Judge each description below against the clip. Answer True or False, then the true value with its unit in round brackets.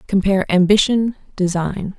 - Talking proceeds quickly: False (90 wpm)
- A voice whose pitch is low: False (195 Hz)